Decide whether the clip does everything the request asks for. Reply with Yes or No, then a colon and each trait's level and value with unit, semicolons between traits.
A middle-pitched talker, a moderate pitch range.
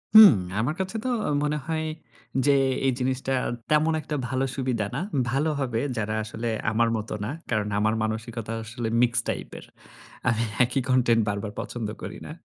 No: low, 120 Hz; average, 3.5 semitones